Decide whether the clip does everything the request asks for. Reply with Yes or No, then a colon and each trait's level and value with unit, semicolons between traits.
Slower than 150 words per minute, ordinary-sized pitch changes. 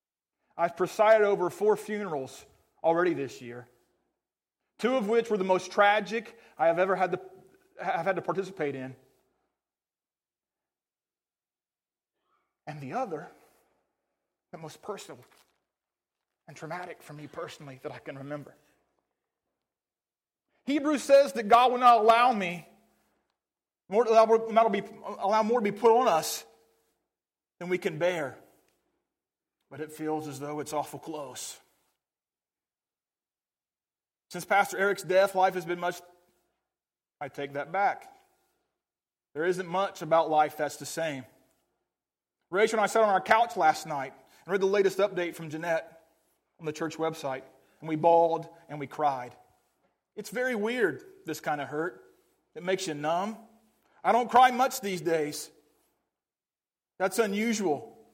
No: average, 140 wpm; wide, 6.0 semitones